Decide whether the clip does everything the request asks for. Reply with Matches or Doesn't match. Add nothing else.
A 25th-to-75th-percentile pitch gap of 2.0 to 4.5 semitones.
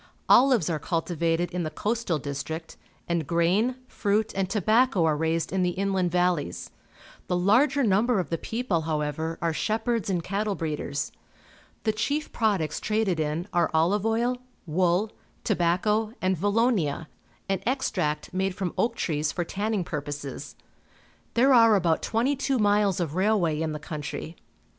Doesn't match